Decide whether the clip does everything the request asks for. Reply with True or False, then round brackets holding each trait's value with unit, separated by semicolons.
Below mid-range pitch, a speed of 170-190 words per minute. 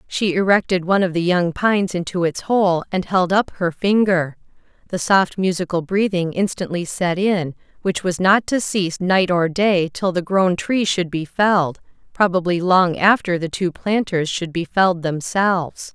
False (180 Hz; 175 wpm)